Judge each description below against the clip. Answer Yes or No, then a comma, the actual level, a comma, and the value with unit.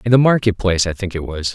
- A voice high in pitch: No, low, 100 Hz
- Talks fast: Yes, fast, 310 wpm